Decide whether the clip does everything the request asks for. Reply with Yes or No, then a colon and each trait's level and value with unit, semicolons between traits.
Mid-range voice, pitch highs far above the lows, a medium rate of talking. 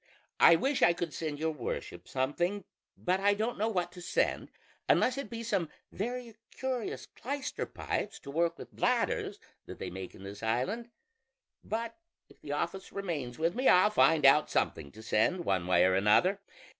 Yes: medium, 175 Hz; wide, 8.2 semitones; average, 180 wpm